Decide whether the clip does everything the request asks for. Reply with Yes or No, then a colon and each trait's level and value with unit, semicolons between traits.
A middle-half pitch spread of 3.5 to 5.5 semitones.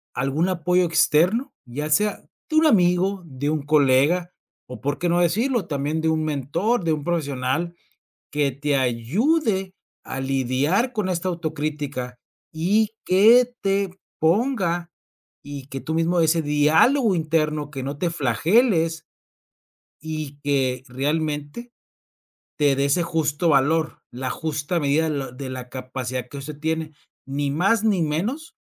Yes: average, 4.2 semitones